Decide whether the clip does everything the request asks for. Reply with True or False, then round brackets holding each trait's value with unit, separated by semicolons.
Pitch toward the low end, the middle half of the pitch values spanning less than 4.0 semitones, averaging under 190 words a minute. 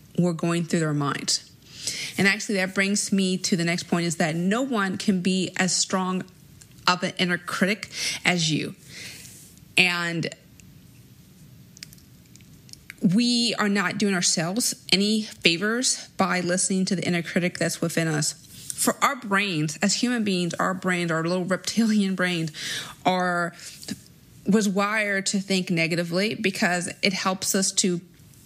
False (185 Hz; 2.6 semitones; 145 wpm)